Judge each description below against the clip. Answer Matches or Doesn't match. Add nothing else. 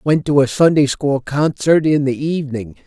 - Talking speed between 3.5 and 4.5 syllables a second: Doesn't match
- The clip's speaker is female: Doesn't match